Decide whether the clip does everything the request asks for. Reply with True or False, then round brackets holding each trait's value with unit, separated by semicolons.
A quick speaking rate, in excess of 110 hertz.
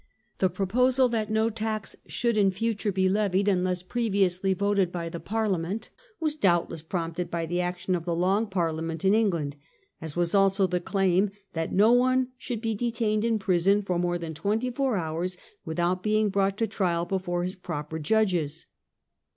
False (175 wpm; 190 Hz)